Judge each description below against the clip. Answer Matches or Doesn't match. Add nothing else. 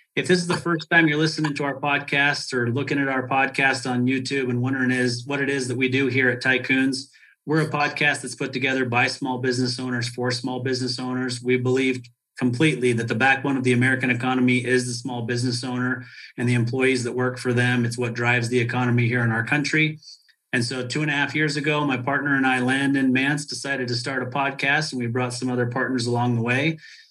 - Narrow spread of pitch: Matches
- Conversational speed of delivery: Doesn't match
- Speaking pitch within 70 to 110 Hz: Doesn't match